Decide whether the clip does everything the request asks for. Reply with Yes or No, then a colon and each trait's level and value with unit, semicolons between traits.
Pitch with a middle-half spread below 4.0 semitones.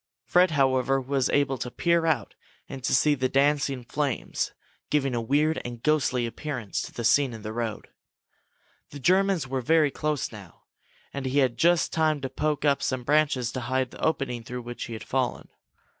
Yes: average, 3.4 semitones